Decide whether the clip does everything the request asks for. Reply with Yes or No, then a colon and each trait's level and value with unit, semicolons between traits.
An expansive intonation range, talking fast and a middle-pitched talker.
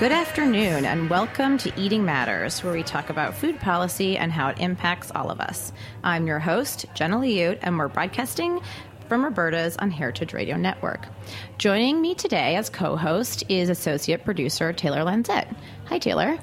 No: wide, 6.1 semitones; average, 170 wpm; medium, 175 Hz